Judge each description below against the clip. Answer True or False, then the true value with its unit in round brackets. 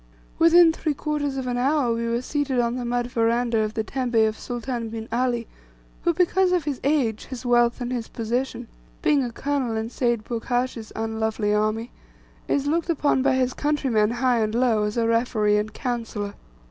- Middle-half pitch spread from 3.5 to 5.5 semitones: False (3.0 semitones)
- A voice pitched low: False (245 Hz)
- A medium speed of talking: True (180 wpm)